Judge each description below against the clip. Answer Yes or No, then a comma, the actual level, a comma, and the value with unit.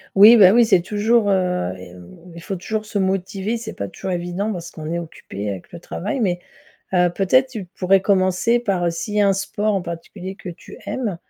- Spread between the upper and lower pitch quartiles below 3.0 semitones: No, average, 3.3 semitones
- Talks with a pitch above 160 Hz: Yes, high, 190 Hz